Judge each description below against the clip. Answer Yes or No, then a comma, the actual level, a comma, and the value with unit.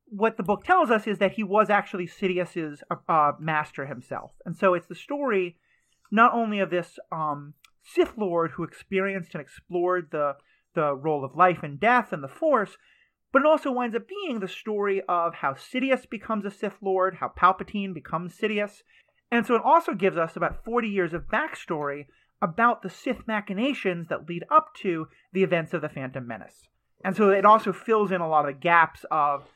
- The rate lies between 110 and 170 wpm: No, average, 195 wpm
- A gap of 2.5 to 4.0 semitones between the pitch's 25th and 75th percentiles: No, average, 4.7 semitones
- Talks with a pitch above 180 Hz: Yes, high, 190 Hz